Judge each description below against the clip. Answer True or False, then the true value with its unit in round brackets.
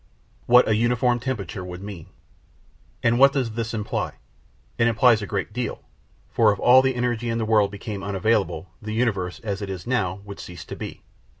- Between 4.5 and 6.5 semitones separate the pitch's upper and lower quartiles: False (3.3 semitones)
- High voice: False (110 Hz)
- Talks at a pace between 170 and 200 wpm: True (190 wpm)